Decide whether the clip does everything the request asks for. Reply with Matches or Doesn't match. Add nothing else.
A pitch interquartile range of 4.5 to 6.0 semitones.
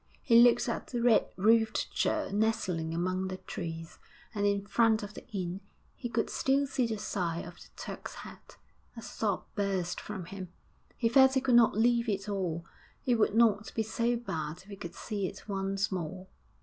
Doesn't match